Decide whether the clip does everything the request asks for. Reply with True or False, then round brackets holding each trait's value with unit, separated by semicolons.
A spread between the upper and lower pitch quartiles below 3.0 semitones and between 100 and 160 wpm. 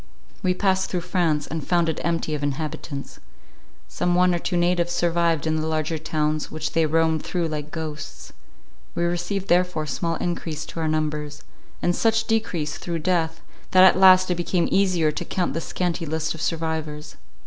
False (2.4 semitones; 180 wpm)